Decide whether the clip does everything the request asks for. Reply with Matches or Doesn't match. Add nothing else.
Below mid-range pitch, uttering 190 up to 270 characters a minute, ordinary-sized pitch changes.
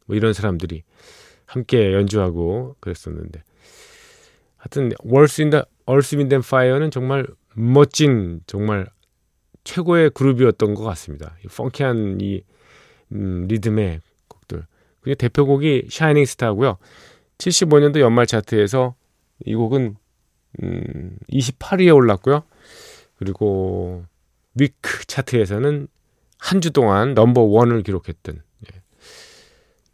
Doesn't match